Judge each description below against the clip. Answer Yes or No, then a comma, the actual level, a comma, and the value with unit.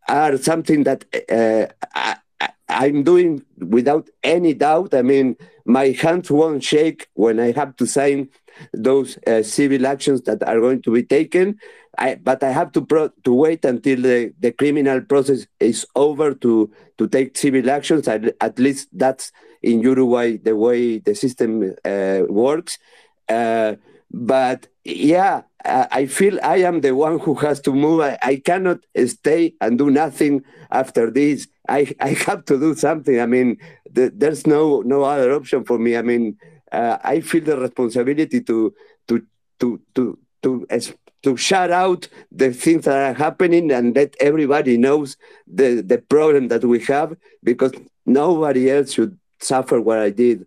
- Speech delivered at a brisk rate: No, average, 165 wpm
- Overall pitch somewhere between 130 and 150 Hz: Yes, low, 135 Hz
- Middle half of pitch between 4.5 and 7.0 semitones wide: No, average, 4.1 semitones